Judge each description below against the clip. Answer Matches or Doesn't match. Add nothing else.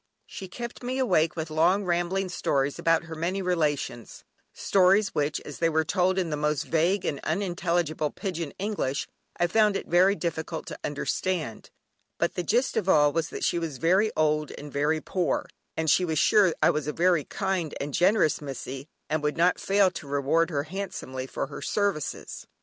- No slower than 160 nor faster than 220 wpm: Matches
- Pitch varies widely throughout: Doesn't match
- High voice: Doesn't match